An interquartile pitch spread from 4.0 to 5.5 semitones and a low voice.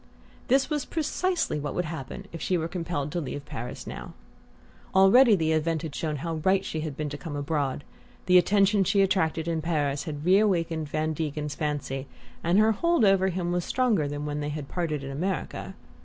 No: average, 4.5 semitones; medium, 165 Hz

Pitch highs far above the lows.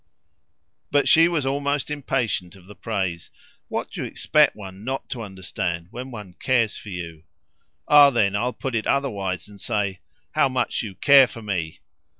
Yes: wide, 5.9 semitones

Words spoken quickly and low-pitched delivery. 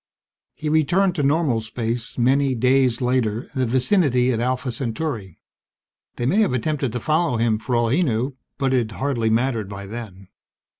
No: average, 170 wpm; low, 125 Hz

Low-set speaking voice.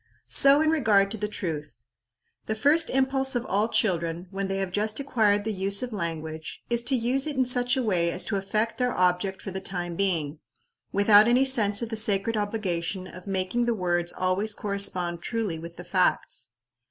No: high, 200 Hz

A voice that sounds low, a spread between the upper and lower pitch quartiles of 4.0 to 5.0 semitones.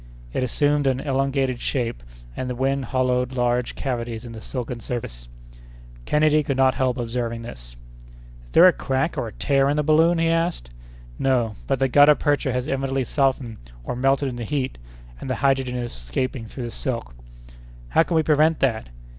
No: low, 130 Hz; average, 2.7 semitones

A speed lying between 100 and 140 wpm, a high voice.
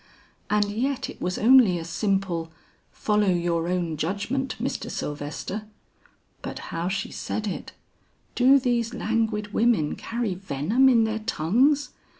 Yes: slow, 135 wpm; high, 210 Hz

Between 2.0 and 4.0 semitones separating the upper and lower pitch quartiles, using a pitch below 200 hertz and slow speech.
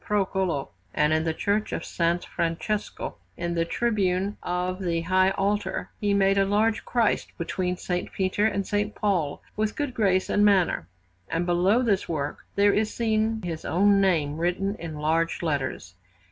No: average, 3.5 semitones; medium, 185 Hz; average, 165 wpm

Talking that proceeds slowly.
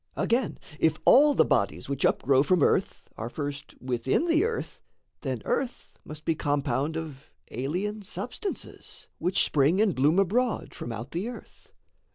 No: average, 155 wpm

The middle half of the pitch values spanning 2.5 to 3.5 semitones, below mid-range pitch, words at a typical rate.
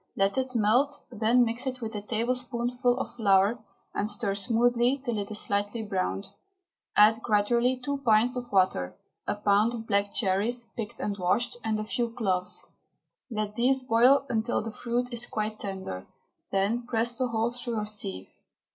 No: average, 2.9 semitones; high, 225 Hz; average, 170 wpm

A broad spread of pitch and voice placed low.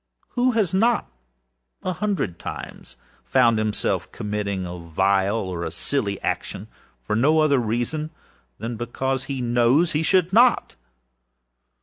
Yes: wide, 7.5 semitones; low, 120 Hz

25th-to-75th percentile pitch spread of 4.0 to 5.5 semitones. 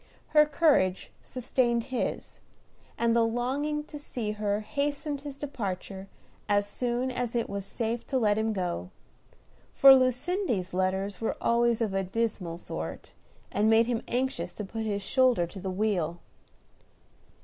Yes: average, 4.5 semitones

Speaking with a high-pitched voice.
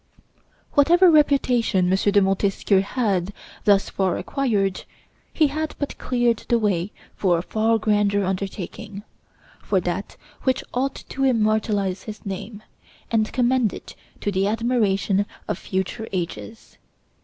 Yes: high, 210 Hz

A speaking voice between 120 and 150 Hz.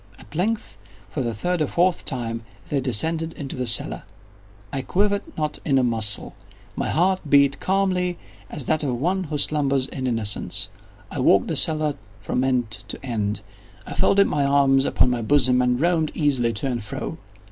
Yes: medium, 140 Hz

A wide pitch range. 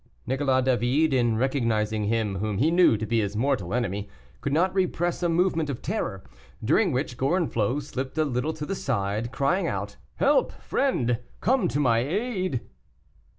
Yes: wide, 6.1 semitones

